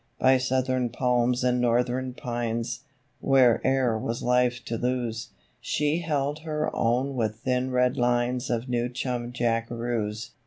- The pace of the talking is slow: Yes, slow, 130 wpm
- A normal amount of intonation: No, narrow, 1.5 semitones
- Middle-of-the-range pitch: No, low, 125 Hz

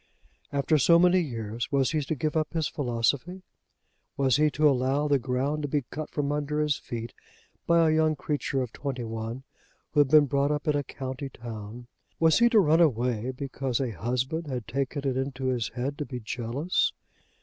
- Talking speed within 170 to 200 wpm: Yes, average, 195 wpm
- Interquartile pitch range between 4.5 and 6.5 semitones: No, average, 3.3 semitones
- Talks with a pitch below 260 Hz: Yes, medium, 140 Hz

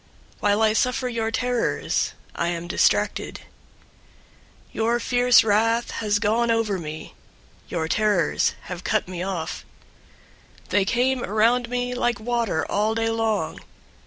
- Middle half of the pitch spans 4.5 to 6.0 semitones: No, average, 3.3 semitones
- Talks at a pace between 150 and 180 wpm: No, slow, 135 wpm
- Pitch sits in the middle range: No, high, 220 Hz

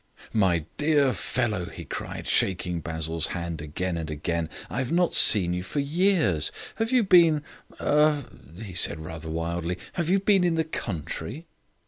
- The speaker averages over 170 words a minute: No, average, 165 wpm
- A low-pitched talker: Yes, very low, 95 Hz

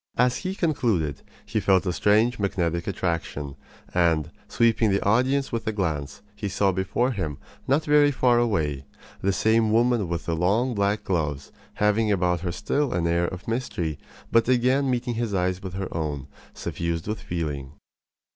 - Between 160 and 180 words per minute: Yes, average, 165 wpm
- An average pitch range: No, wide, 5.8 semitones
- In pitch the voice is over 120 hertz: No, low, 100 Hz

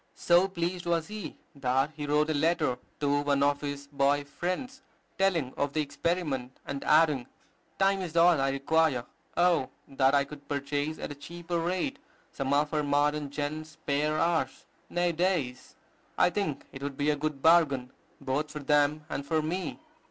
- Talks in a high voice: No, medium, 150 Hz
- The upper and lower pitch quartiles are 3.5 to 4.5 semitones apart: No, average, 3.1 semitones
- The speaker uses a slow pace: No, average, 175 wpm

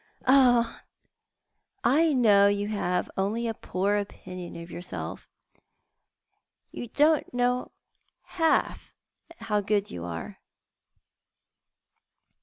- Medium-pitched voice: No, high, 210 Hz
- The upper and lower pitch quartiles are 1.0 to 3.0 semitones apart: No, average, 4.2 semitones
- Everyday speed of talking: No, slow, 95 wpm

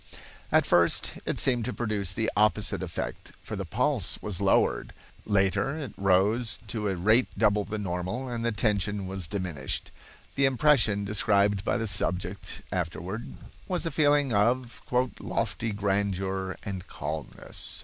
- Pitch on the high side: No, low, 100 Hz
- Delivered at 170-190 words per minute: No, average, 145 wpm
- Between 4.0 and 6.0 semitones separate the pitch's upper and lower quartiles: No, average, 3.4 semitones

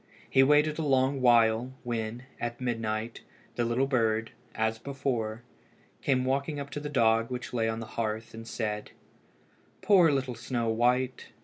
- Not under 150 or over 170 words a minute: Yes, average, 155 wpm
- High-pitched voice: No, low, 120 Hz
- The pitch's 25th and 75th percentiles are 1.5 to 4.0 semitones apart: Yes, average, 2.9 semitones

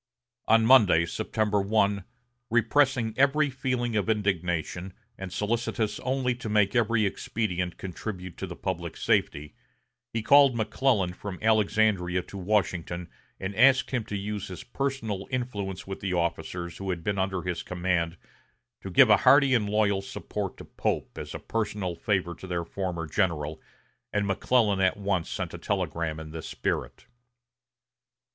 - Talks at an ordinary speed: Yes, average, 150 wpm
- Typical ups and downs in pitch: Yes, average, 3.9 semitones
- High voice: No, low, 100 Hz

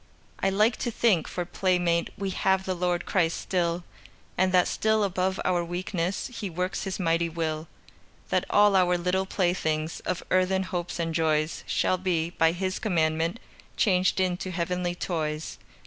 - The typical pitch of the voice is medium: Yes, medium, 180 Hz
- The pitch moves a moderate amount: No, narrow, 1.9 semitones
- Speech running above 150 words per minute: Yes, average, 160 wpm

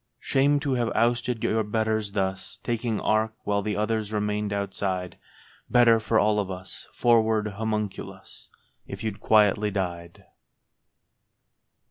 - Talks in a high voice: No, low, 105 Hz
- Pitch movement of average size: No, narrow, 1.9 semitones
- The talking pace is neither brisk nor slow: No, slow, 125 wpm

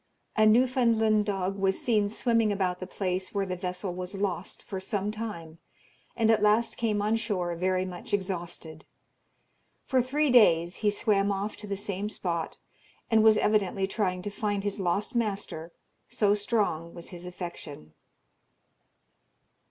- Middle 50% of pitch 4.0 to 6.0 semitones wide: No, average, 2.9 semitones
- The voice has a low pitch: No, high, 200 Hz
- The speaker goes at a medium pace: Yes, average, 150 wpm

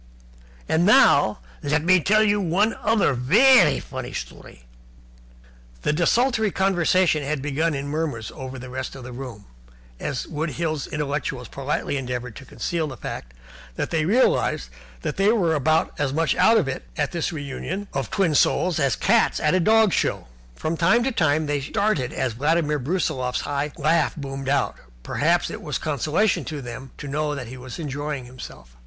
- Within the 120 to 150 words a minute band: No, average, 180 wpm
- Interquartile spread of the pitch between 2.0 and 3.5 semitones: No, average, 4.7 semitones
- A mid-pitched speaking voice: Yes, medium, 150 Hz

